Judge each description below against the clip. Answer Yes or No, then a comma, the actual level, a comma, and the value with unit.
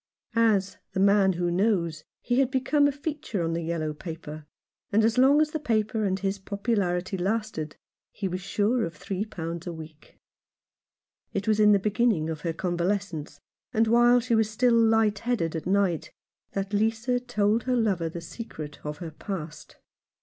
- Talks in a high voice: Yes, high, 200 Hz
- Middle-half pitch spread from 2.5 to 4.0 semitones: No, average, 5.0 semitones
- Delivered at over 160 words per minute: Yes, average, 180 wpm